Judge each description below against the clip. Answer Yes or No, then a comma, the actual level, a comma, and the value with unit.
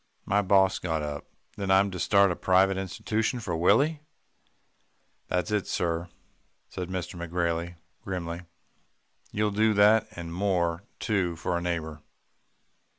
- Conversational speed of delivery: No, slow, 130 wpm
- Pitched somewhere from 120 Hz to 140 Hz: No, very low, 95 Hz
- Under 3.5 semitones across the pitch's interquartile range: Yes, average, 2.8 semitones